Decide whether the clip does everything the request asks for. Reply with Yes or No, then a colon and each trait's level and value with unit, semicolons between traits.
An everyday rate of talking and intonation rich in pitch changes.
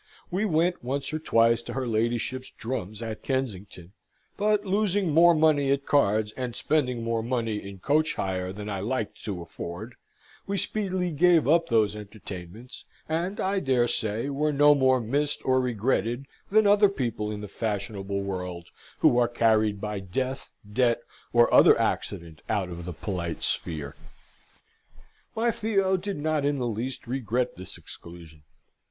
Yes: average, 160 wpm; wide, 6.4 semitones